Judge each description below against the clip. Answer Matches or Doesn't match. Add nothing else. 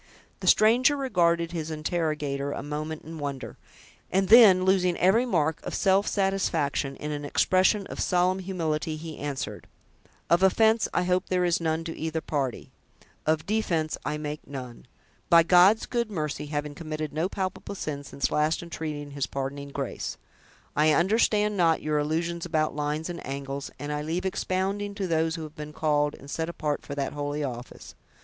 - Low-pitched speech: Doesn't match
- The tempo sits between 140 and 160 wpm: Doesn't match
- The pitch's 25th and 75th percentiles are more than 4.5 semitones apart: Doesn't match